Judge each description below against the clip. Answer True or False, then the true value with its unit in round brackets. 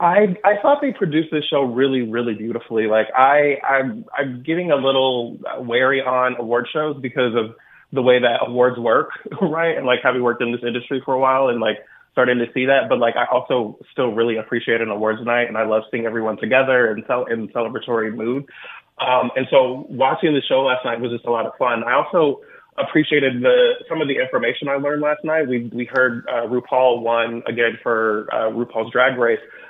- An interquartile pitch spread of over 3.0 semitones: True (4.1 semitones)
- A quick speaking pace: True (210 wpm)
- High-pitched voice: False (125 Hz)